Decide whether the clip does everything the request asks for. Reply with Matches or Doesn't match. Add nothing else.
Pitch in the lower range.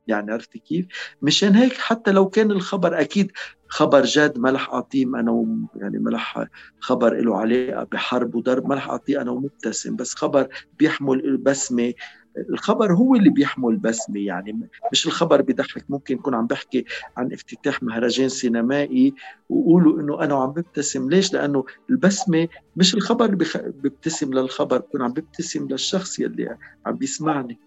Doesn't match